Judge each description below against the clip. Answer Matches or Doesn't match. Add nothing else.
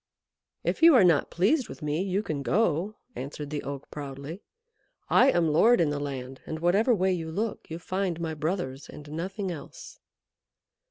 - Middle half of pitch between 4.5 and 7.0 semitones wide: Matches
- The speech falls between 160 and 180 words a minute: Matches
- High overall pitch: Doesn't match